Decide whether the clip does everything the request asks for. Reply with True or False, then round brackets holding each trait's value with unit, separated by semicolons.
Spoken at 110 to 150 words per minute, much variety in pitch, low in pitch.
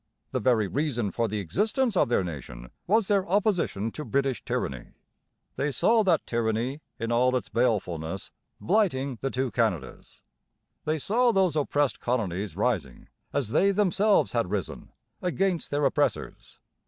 True (145 wpm; 8.9 semitones; 130 Hz)